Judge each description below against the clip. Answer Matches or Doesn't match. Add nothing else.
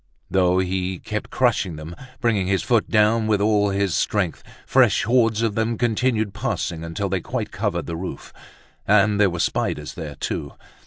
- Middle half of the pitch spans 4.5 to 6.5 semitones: Doesn't match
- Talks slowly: Doesn't match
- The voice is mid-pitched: Doesn't match